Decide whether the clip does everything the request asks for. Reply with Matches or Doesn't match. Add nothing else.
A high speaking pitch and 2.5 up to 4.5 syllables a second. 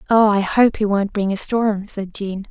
Matches